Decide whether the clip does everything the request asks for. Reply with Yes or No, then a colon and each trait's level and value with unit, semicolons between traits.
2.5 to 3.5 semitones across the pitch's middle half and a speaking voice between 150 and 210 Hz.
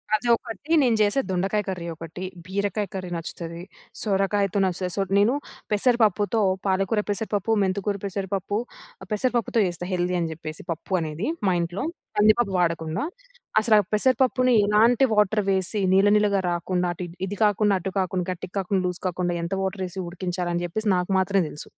Yes: average, 2.9 semitones; high, 195 Hz